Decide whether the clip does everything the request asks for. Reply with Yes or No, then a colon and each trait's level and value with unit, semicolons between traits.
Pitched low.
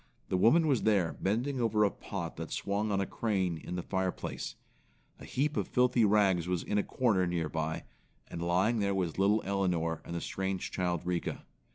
Yes: very low, 95 Hz